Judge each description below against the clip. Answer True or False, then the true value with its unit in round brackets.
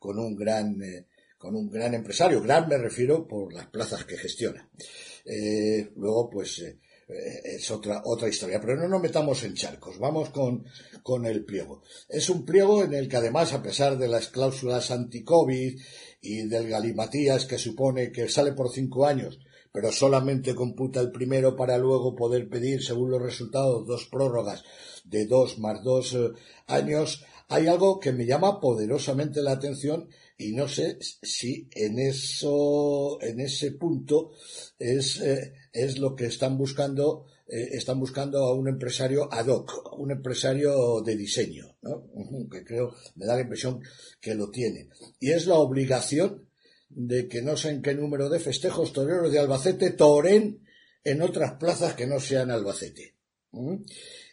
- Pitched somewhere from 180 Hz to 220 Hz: False (130 Hz)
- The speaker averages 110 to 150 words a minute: False (165 wpm)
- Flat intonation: False (3.3 semitones)